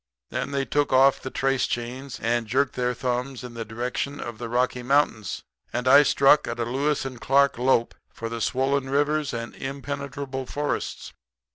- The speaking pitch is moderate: No, low, 130 Hz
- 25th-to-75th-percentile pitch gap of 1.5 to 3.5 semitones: Yes, narrow, 2.5 semitones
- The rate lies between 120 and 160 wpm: No, average, 170 wpm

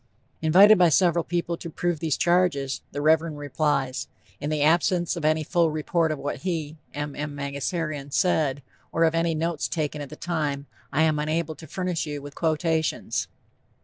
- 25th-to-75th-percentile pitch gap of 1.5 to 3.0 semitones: Yes, narrow, 2.4 semitones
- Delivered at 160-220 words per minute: Yes, average, 180 wpm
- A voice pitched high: No, medium, 155 Hz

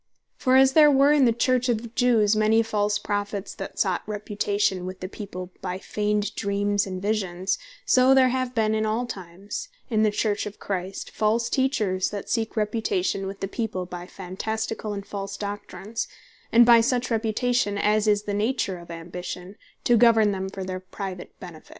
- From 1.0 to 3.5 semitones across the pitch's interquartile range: Yes, average, 2.9 semitones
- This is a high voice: Yes, high, 210 Hz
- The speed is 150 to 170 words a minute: No, average, 180 wpm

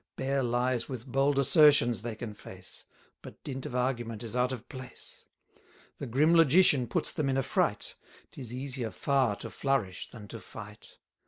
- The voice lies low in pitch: Yes, low, 125 Hz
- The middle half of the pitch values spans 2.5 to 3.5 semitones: Yes, average, 2.9 semitones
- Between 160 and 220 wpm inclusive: Yes, average, 175 wpm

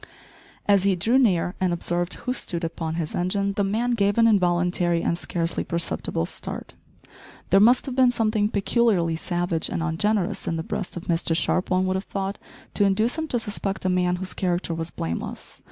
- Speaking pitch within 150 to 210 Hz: Yes, medium, 185 Hz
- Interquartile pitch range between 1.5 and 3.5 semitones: Yes, average, 3.2 semitones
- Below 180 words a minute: No, average, 190 wpm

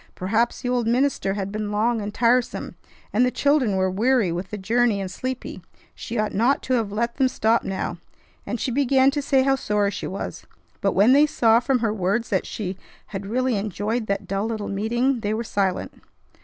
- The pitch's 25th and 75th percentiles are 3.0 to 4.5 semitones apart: Yes, average, 3.8 semitones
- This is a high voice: Yes, high, 225 Hz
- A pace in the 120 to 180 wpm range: No, fast, 205 wpm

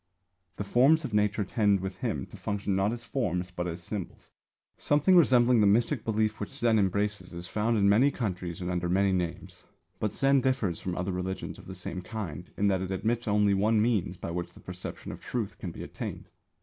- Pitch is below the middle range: Yes, low, 100 Hz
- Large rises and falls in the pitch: No, average, 3.8 semitones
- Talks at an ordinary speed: No, fast, 210 wpm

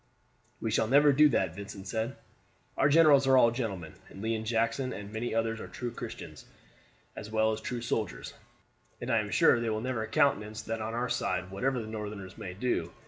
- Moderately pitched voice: No, low, 110 Hz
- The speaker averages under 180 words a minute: No, average, 200 wpm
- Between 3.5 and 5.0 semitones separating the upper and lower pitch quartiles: No, average, 2.9 semitones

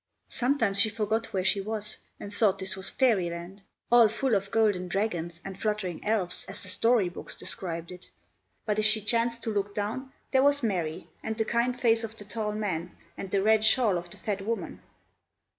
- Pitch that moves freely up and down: No, average, 3.0 semitones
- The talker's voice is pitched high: Yes, high, 210 Hz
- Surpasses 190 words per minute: Yes, average, 200 wpm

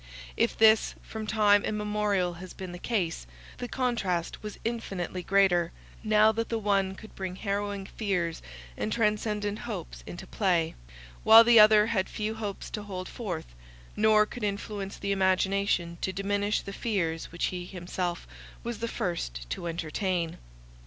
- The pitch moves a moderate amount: Yes, average, 3.0 semitones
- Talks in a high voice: Yes, high, 200 Hz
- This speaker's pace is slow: No, average, 150 wpm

